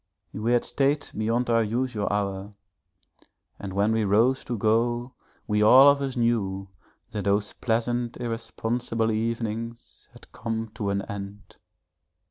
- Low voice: Yes, low, 115 Hz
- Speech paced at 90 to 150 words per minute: Yes, slow, 135 wpm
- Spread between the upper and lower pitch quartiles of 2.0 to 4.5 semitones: Yes, narrow, 2.6 semitones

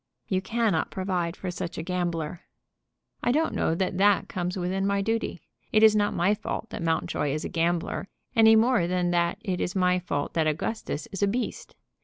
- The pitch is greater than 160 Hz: Yes, medium, 185 Hz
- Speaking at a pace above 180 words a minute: Yes, average, 195 wpm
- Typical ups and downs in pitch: Yes, average, 3.2 semitones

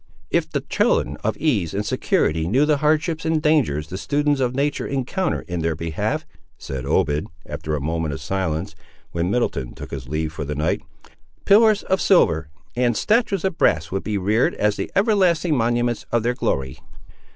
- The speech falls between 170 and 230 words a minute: Yes, average, 180 wpm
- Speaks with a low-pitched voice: Yes, low, 110 Hz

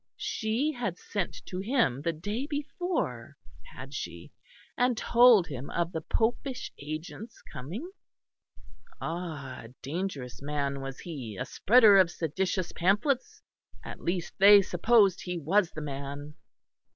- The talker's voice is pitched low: No, medium, 180 Hz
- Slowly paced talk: Yes, slow, 130 wpm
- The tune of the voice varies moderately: No, wide, 7.5 semitones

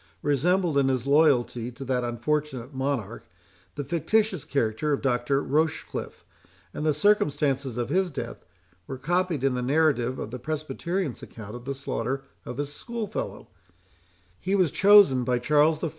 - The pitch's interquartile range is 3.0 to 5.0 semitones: Yes, average, 4.1 semitones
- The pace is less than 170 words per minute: Yes, average, 155 wpm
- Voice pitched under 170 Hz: Yes, medium, 140 Hz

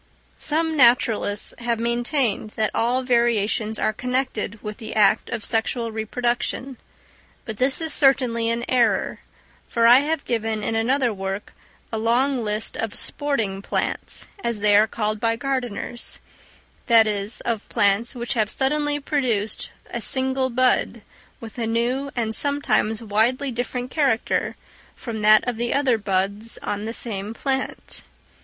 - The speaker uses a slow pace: No, average, 145 wpm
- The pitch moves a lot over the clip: No, average, 3.0 semitones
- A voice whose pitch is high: Yes, high, 235 Hz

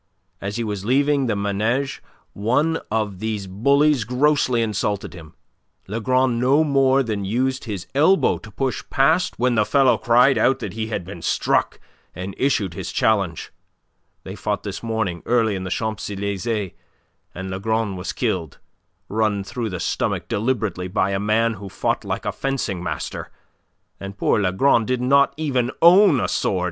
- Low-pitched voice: Yes, low, 110 Hz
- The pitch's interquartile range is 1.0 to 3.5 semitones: No, average, 4.8 semitones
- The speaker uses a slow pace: No, average, 165 wpm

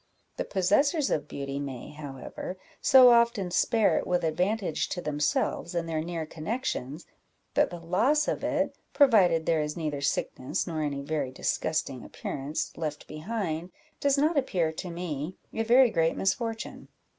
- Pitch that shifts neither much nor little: No, wide, 6.8 semitones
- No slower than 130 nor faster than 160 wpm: Yes, average, 155 wpm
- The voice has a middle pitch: Yes, medium, 170 Hz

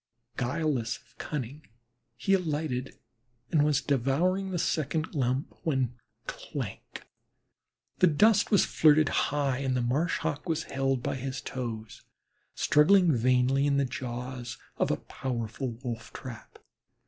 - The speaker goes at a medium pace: No, slow, 130 wpm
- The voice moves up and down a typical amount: Yes, average, 3.7 semitones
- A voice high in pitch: No, low, 135 Hz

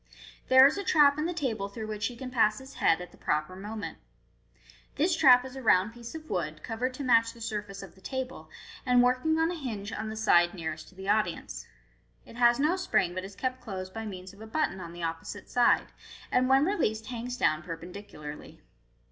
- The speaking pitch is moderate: No, high, 225 Hz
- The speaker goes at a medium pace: No, fast, 215 wpm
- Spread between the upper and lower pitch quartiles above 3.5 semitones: Yes, average, 5.3 semitones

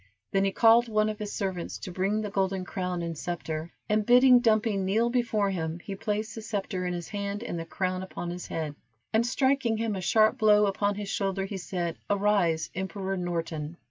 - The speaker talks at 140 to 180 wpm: No, fast, 205 wpm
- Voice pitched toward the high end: Yes, high, 195 Hz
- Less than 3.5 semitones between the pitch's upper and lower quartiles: Yes, average, 3.1 semitones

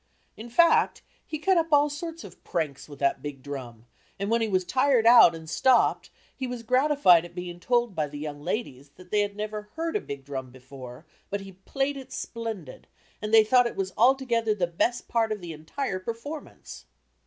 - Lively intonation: Yes, wide, 7.6 semitones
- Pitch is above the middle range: Yes, high, 210 Hz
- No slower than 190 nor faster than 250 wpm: Yes, average, 200 wpm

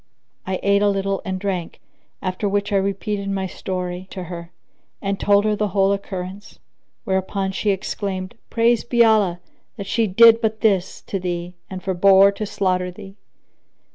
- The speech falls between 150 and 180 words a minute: Yes, average, 165 wpm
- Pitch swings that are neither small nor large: No, narrow, 1.6 semitones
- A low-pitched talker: No, high, 195 Hz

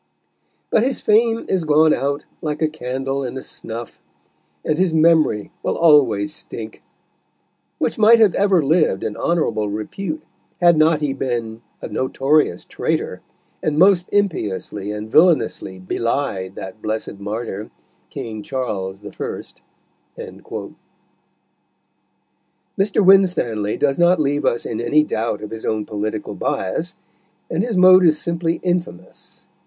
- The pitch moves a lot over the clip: Yes, wide, 7.8 semitones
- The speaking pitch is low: No, medium, 145 Hz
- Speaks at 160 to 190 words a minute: No, slow, 135 wpm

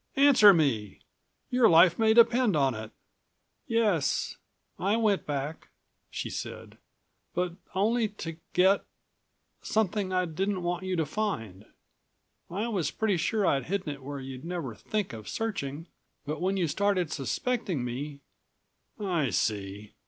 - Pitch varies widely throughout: Yes, wide, 6.6 semitones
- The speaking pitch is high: No, medium, 180 Hz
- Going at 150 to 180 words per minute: No, average, 140 wpm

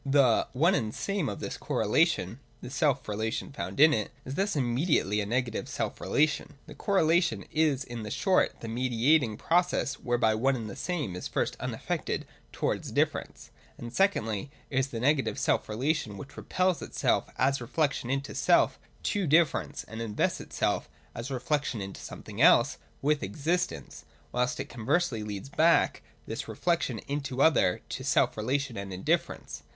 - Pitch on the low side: Yes, low, 130 Hz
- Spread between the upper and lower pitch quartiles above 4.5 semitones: Yes, wide, 5.5 semitones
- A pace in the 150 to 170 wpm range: Yes, average, 165 wpm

